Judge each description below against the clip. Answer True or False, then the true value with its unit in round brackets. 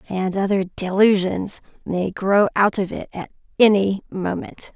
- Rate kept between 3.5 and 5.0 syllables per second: True (4.1 syllables/s)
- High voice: True (195 Hz)